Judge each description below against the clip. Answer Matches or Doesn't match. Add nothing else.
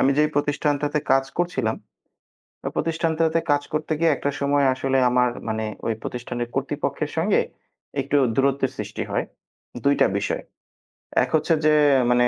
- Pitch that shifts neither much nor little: Matches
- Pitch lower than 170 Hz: Matches